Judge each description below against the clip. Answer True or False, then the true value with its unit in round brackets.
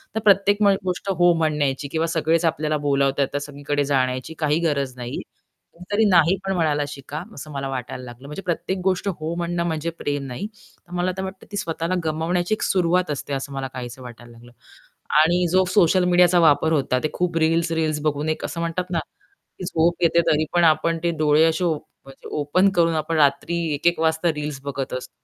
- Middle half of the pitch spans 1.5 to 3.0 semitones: False (3.4 semitones)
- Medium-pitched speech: True (160 Hz)